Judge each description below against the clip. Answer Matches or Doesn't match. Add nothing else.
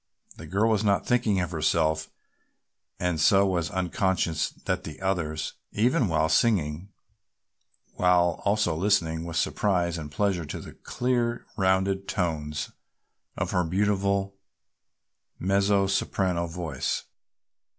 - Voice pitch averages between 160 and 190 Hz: Doesn't match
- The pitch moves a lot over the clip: Doesn't match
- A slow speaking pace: Matches